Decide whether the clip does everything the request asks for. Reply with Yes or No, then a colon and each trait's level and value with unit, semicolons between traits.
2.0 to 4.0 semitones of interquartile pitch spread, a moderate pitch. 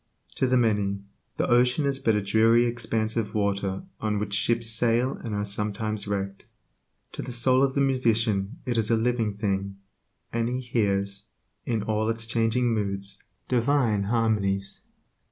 No: average, 2.9 semitones; low, 110 Hz